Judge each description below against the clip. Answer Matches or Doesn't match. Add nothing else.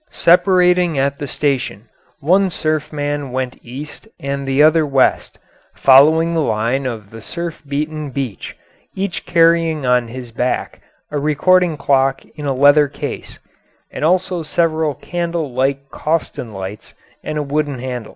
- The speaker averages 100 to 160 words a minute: Matches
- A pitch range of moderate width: Matches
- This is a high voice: Doesn't match